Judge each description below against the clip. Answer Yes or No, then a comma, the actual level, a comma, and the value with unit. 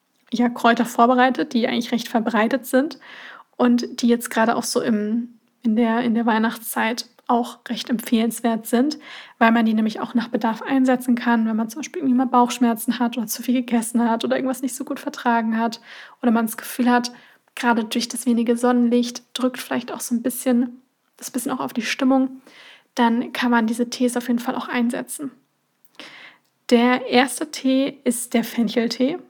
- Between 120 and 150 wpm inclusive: No, average, 185 wpm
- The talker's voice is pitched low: No, high, 245 Hz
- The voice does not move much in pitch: Yes, narrow, 1.7 semitones